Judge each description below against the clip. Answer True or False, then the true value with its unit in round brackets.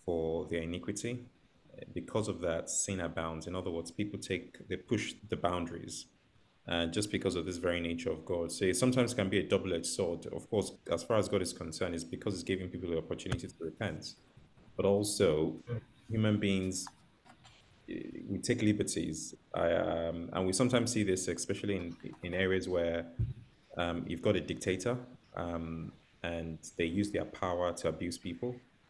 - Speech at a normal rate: True (175 wpm)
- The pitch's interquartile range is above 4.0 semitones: False (3.7 semitones)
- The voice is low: True (95 Hz)